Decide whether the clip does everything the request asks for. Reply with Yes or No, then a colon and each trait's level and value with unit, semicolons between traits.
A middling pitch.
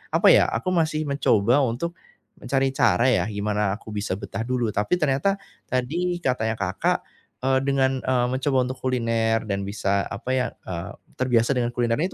No: low, 125 Hz